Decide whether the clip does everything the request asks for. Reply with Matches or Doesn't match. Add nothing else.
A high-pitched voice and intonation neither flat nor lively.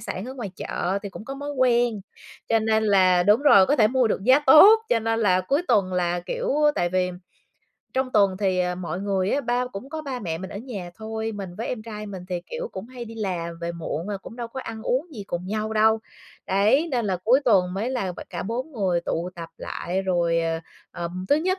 Matches